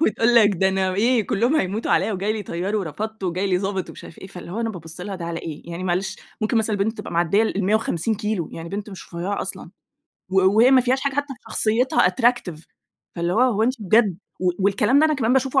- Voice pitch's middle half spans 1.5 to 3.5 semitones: No, average, 3.9 semitones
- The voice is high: Yes, high, 205 Hz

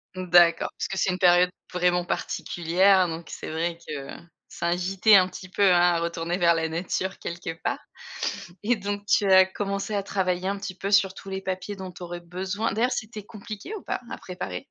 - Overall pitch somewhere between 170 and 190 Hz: Yes, medium, 185 Hz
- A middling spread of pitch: No, narrow, 2.3 semitones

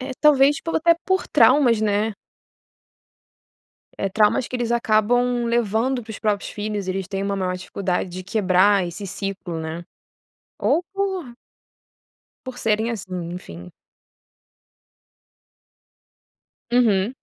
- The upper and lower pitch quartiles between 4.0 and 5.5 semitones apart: Yes, average, 4.3 semitones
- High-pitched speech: Yes, high, 215 Hz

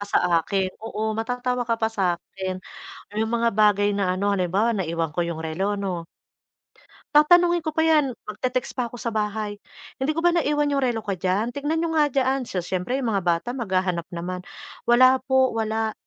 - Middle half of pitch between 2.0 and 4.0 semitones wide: No, wide, 5.6 semitones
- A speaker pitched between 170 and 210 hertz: No, high, 220 Hz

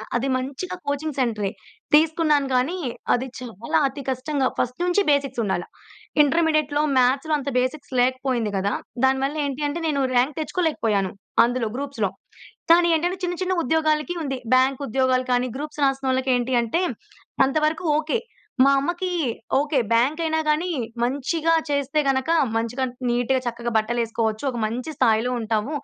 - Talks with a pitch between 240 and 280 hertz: Yes, very high, 270 Hz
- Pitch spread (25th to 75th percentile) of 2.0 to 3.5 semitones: No, average, 3.9 semitones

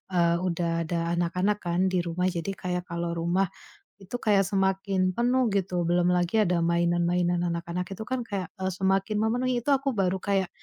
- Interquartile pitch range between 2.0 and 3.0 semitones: Yes, narrow, 2.4 semitones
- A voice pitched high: No, medium, 180 Hz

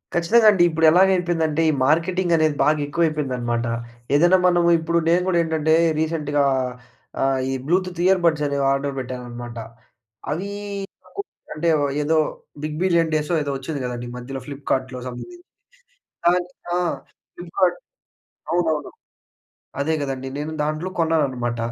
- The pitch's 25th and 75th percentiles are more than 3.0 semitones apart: Yes, average, 3.9 semitones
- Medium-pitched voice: Yes, medium, 155 Hz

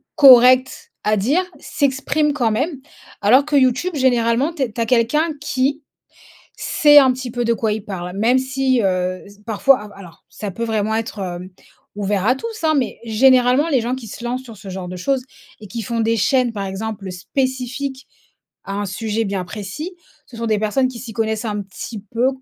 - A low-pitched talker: No, high, 235 Hz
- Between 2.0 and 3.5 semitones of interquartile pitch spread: No, average, 4.1 semitones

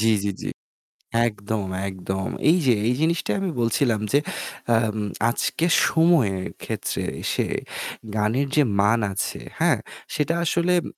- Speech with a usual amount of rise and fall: No, wide, 7.6 semitones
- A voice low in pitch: Yes, low, 115 Hz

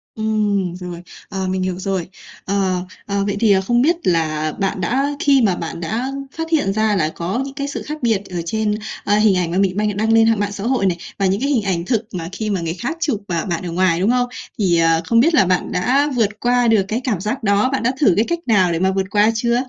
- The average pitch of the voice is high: Yes, high, 205 Hz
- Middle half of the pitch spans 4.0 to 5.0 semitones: Yes, average, 4.4 semitones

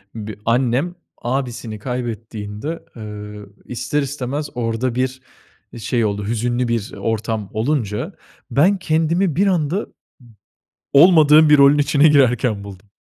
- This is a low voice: Yes, low, 125 Hz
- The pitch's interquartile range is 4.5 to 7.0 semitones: Yes, average, 5.0 semitones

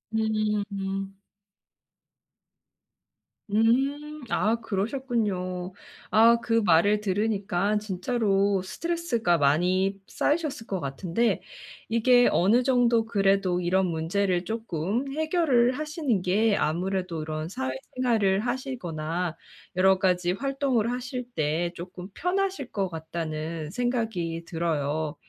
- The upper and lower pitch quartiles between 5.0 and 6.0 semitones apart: Yes, average, 5.3 semitones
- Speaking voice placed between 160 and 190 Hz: No, high, 200 Hz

